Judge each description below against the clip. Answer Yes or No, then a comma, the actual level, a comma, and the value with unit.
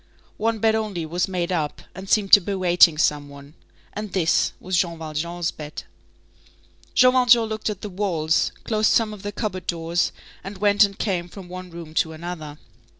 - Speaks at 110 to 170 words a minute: No, average, 185 wpm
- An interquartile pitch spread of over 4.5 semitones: No, average, 4.0 semitones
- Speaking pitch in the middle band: Yes, medium, 180 Hz